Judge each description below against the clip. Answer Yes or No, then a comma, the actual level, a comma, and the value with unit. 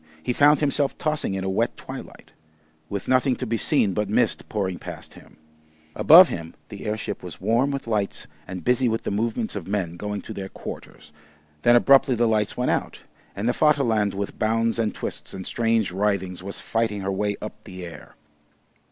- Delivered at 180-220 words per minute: Yes, average, 190 wpm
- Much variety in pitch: No, average, 3.7 semitones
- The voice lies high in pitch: No, low, 105 Hz